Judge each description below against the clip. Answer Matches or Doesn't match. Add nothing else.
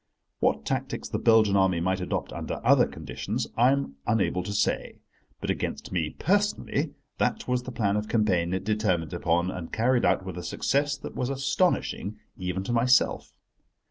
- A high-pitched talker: Doesn't match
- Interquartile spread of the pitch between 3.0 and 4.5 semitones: Doesn't match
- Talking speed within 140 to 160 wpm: Doesn't match